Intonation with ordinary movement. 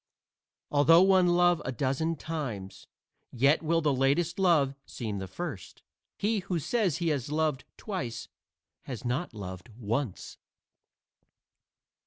No: wide, 5.9 semitones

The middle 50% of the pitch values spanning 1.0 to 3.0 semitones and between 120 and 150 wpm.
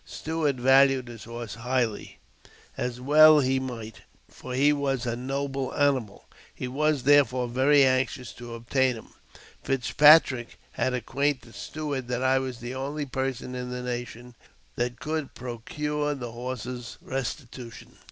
Yes: narrow, 2.4 semitones; average, 140 wpm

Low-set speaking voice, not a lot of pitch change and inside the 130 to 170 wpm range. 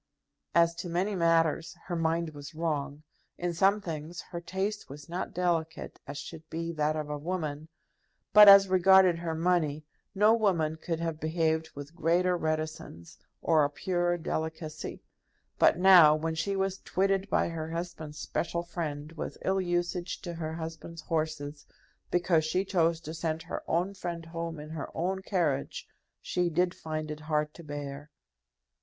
No: medium, 165 Hz; narrow, 2.2 semitones; average, 160 wpm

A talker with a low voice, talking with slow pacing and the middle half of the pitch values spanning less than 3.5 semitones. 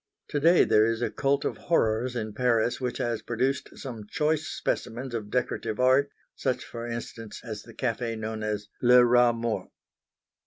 No: low, 120 Hz; average, 170 wpm; narrow, 2.4 semitones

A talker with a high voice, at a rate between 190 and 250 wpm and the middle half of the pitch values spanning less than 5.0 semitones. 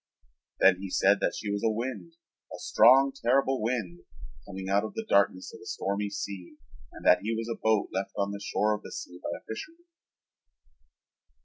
No: low, 105 Hz; average, 195 wpm; average, 3.3 semitones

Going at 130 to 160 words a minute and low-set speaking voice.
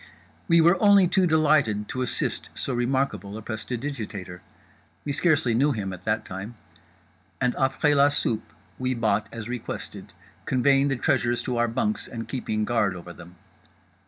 Yes: average, 150 wpm; low, 120 Hz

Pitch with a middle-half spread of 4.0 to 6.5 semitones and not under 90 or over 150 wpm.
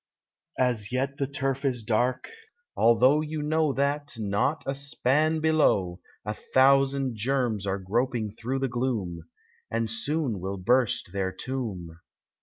Yes: average, 4.6 semitones; average, 140 wpm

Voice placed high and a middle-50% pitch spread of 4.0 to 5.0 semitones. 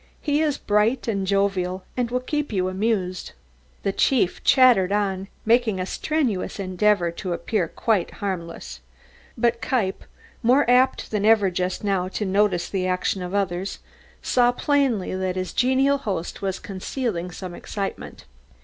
Yes: high, 200 Hz; average, 4.4 semitones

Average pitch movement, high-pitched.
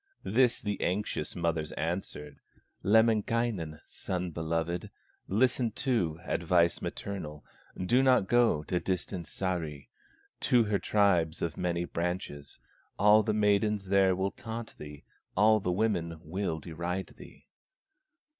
No: average, 4.1 semitones; very low, 95 Hz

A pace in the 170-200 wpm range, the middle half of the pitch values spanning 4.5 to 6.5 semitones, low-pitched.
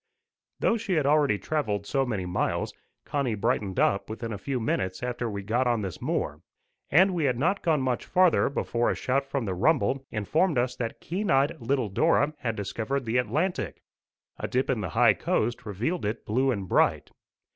Yes: average, 190 wpm; wide, 5.4 semitones; low, 125 Hz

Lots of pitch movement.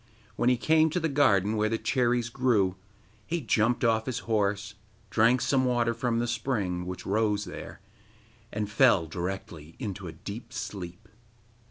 No: average, 3.8 semitones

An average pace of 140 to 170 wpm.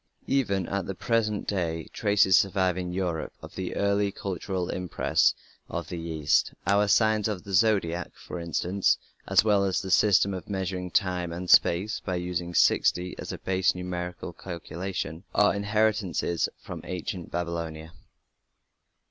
Yes: average, 150 wpm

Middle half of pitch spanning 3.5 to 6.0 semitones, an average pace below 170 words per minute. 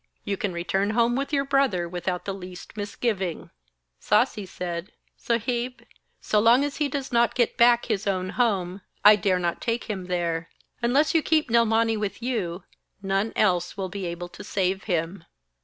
No: average, 4.6 semitones; average, 175 wpm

